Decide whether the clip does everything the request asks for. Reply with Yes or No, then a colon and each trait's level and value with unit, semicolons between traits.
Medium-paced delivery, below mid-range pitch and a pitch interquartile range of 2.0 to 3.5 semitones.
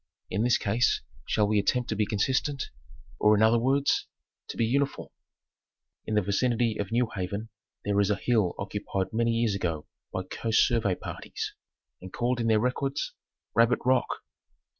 Yes: average, 170 wpm; low, 110 Hz; average, 3.1 semitones